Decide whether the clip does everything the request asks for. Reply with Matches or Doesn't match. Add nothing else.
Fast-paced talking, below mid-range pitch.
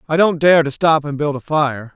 Doesn't match